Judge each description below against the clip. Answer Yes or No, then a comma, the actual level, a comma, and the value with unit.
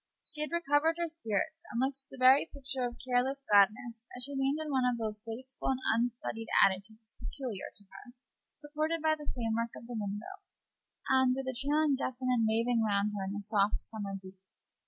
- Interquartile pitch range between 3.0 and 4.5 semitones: Yes, average, 4.1 semitones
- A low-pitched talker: No, high, 245 Hz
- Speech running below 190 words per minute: No, average, 195 wpm